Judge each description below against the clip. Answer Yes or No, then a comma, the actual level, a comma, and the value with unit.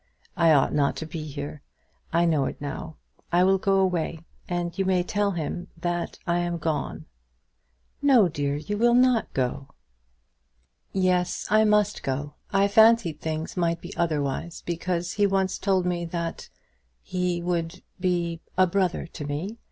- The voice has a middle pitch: Yes, medium, 175 Hz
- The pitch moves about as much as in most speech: Yes, average, 3.0 semitones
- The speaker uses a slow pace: No, average, 160 wpm